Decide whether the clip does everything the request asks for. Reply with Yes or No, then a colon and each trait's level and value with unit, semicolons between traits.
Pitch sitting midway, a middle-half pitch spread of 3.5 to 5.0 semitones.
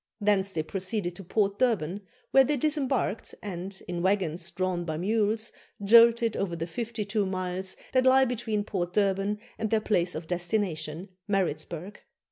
No: high, 195 Hz; average, 3.8 semitones